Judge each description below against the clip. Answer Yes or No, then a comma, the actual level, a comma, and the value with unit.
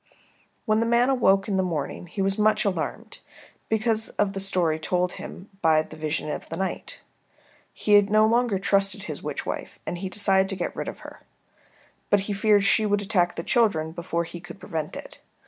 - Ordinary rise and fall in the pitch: Yes, average, 3.3 semitones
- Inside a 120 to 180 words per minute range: No, average, 200 wpm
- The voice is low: No, high, 195 Hz